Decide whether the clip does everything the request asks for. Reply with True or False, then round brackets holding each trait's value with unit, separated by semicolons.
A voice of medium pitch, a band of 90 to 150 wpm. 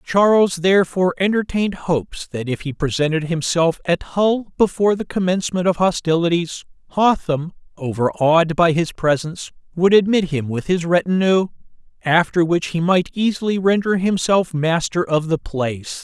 True (175 Hz; 140 wpm)